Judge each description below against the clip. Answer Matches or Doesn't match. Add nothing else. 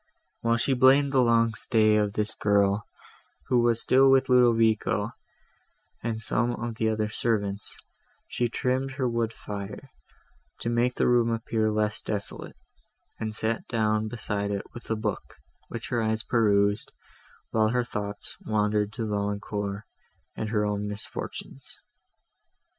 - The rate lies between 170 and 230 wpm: Doesn't match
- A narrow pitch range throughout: Matches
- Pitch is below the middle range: Matches